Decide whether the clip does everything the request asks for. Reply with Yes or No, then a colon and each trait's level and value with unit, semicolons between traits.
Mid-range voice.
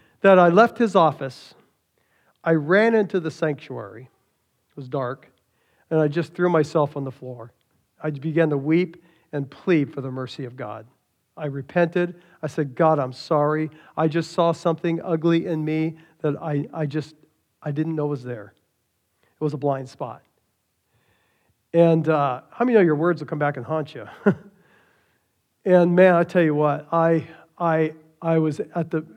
Yes: medium, 155 Hz